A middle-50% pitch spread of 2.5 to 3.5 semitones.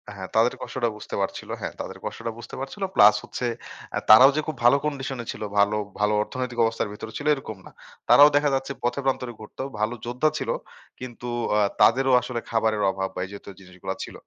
No: average, 3.9 semitones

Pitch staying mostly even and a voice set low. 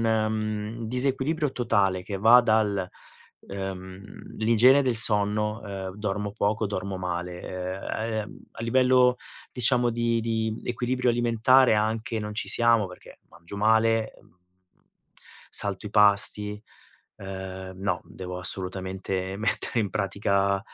No: average, 3.1 semitones; low, 105 Hz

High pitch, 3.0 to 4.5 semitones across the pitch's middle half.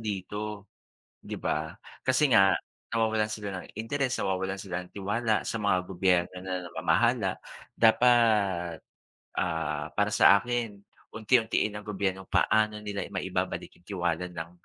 No: low, 100 Hz; average, 3.3 semitones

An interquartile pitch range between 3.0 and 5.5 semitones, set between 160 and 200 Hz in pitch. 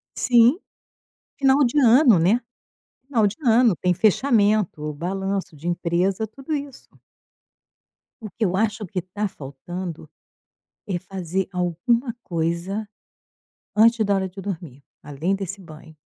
Yes: average, 4.4 semitones; high, 195 Hz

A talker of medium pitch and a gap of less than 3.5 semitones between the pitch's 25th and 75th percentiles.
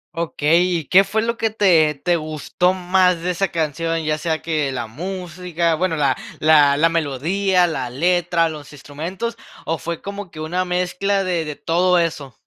Yes: medium, 170 Hz; average, 2.9 semitones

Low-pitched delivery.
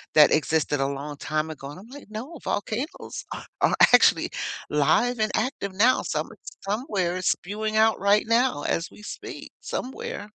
No: high, 205 Hz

